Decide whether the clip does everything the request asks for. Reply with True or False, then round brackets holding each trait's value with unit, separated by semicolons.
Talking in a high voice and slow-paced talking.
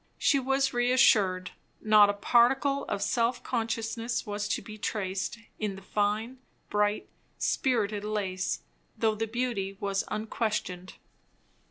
True (215 Hz; 125 wpm)